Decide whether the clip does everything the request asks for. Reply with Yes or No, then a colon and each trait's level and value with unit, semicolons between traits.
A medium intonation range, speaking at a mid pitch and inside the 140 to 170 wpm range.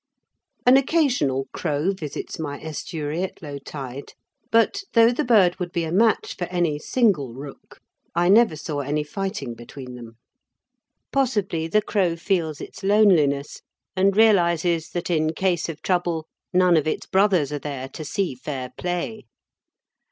Yes: average, 5.0 semitones; medium, 170 Hz; average, 150 wpm